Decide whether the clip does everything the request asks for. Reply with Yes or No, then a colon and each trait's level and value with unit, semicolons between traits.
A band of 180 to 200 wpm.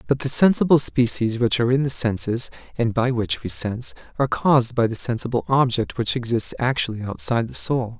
Yes: average, 195 wpm